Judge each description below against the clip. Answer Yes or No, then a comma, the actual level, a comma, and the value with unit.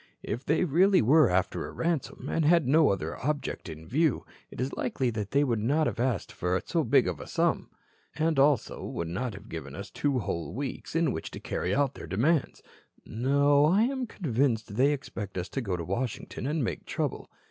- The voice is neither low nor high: No, low, 130 Hz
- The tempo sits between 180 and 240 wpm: Yes, average, 200 wpm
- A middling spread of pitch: No, wide, 6.9 semitones